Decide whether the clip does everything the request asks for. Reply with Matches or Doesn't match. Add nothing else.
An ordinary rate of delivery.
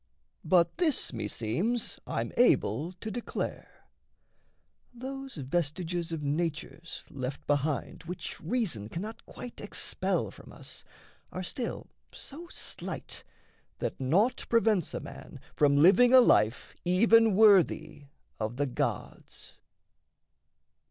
Doesn't match